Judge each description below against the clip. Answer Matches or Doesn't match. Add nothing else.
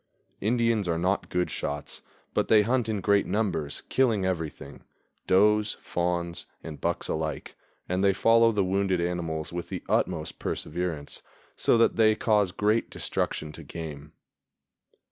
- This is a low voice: Matches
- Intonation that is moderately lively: Matches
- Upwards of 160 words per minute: Doesn't match